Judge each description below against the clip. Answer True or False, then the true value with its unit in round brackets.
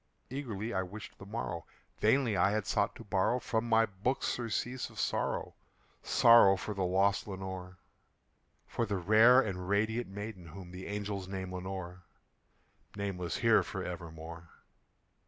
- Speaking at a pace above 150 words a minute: False (145 wpm)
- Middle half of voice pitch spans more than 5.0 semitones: False (3.2 semitones)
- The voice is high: False (100 Hz)